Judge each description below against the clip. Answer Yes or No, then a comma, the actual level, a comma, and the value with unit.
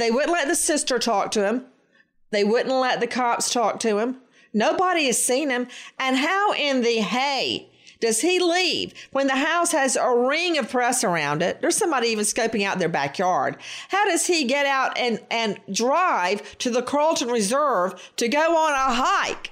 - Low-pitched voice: No, very high, 255 Hz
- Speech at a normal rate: Yes, average, 190 wpm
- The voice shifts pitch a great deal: No, average, 4.9 semitones